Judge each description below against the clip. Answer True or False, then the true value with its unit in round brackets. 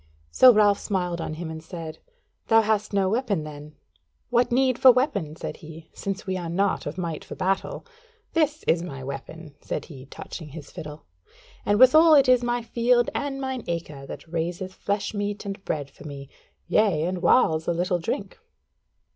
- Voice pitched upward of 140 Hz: True (185 Hz)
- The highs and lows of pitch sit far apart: True (6.4 semitones)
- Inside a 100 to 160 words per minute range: False (180 wpm)